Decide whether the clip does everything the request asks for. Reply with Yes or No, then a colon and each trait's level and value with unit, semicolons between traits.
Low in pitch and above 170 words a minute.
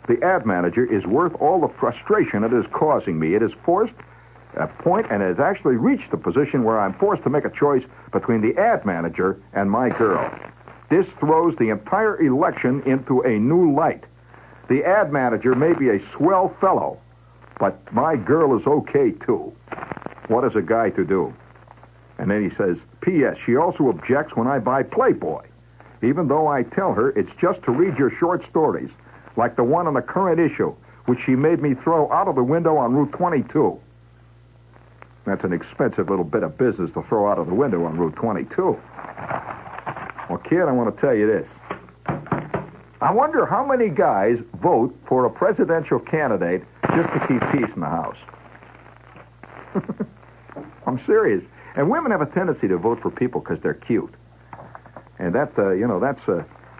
Yes: low, 125 Hz; average, 185 wpm